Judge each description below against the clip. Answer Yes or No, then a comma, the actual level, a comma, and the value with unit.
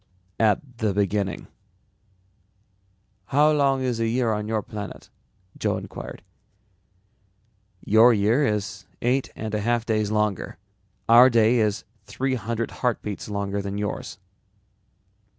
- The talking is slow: Yes, slow, 120 wpm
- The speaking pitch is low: Yes, low, 110 Hz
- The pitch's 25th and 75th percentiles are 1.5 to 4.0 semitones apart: Yes, average, 2.8 semitones